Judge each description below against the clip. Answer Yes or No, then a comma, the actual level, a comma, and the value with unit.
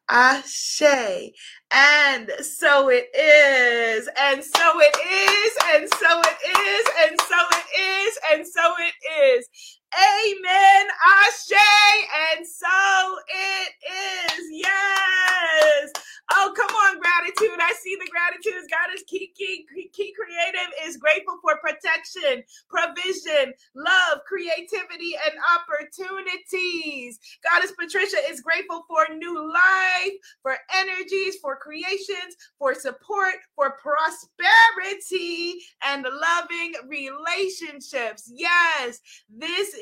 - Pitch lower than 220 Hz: No, very high, 345 Hz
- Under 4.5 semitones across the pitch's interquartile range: Yes, average, 4.1 semitones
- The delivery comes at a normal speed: No, slow, 105 wpm